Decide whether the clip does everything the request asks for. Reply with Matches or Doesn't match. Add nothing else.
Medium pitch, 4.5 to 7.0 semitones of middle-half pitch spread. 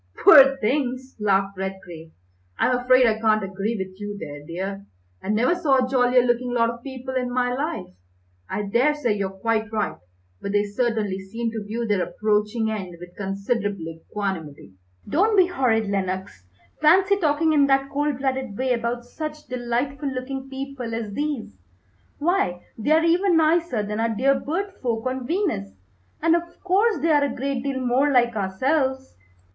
Doesn't match